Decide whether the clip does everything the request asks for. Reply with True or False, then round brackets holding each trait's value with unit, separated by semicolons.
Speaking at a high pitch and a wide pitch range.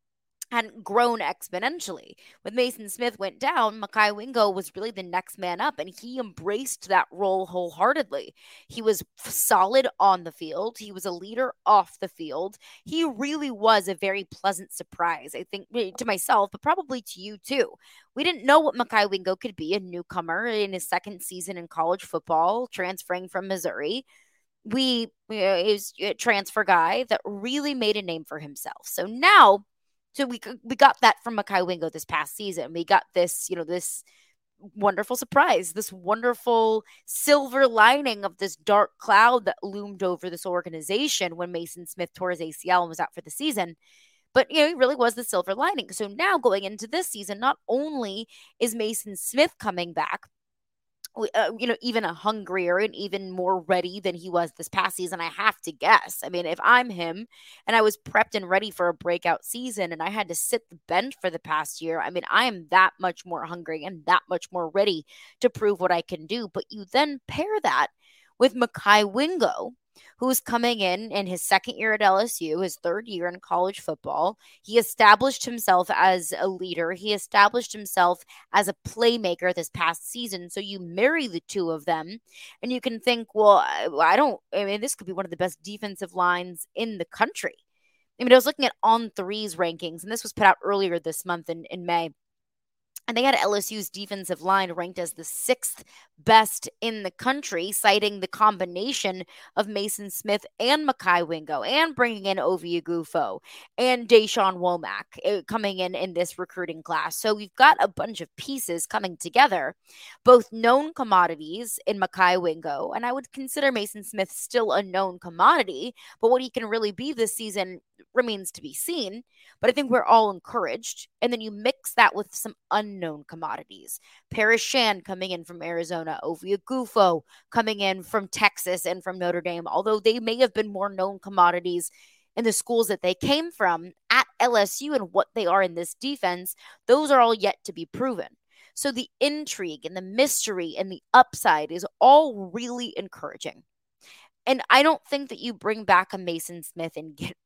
False (200 Hz; 4.8 semitones)